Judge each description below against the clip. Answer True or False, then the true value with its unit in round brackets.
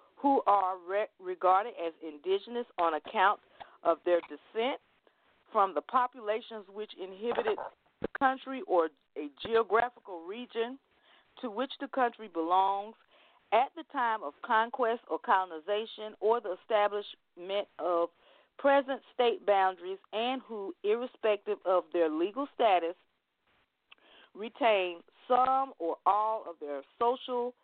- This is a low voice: False (215 Hz)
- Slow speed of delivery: True (120 wpm)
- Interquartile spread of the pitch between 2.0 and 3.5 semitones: False (5.2 semitones)